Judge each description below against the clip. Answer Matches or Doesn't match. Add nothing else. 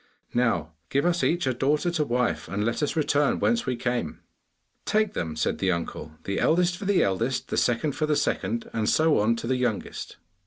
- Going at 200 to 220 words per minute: Matches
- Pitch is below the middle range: Matches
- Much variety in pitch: Matches